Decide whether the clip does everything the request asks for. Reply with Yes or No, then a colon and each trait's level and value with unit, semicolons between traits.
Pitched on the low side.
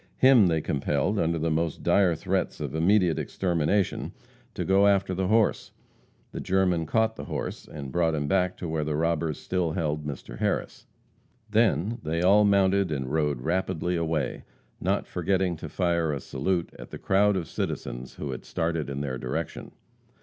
Yes: very low, 85 Hz